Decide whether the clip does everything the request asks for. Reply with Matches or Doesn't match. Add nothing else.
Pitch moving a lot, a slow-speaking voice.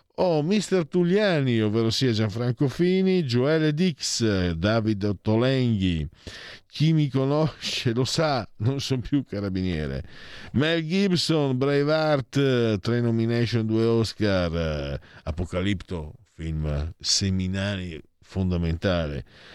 Matches